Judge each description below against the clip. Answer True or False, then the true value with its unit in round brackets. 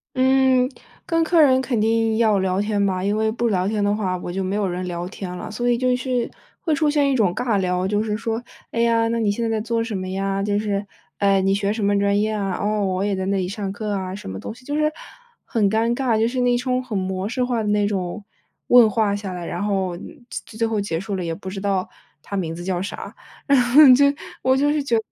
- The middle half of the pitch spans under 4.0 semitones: True (3.6 semitones)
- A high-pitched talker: True (210 Hz)